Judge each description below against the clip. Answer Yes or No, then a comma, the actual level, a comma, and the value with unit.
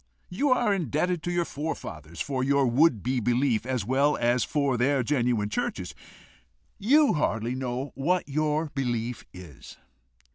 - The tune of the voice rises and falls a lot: No, average, 4.3 semitones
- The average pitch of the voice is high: No, low, 135 Hz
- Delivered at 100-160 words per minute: Yes, average, 145 wpm